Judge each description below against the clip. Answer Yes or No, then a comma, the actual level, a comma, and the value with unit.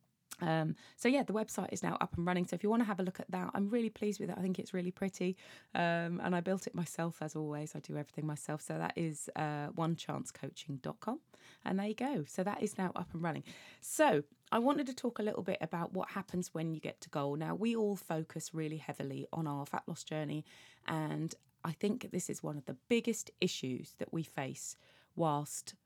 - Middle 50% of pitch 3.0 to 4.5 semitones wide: No, average, 5.0 semitones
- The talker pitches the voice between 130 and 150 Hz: No, medium, 175 Hz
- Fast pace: Yes, fast, 230 wpm